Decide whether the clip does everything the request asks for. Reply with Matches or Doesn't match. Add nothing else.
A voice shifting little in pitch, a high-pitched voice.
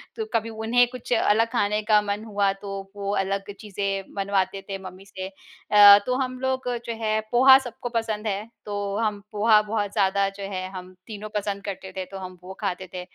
Matches